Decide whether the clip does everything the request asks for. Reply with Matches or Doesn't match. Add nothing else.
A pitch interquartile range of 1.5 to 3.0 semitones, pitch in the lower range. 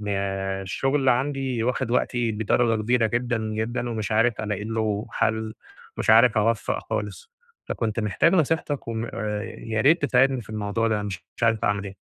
Matches